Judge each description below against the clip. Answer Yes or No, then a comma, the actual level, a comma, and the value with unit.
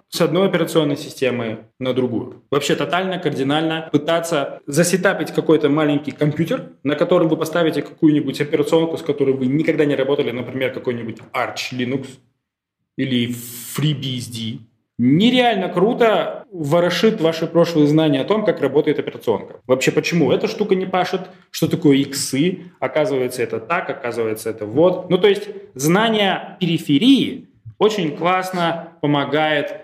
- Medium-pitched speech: Yes, medium, 155 Hz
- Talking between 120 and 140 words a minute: Yes, average, 135 wpm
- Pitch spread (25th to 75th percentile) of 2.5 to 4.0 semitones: No, average, 4.6 semitones